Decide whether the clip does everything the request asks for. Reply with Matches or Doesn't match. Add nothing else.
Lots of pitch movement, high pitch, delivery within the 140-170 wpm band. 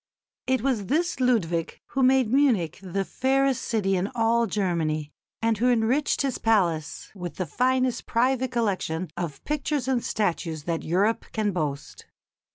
Matches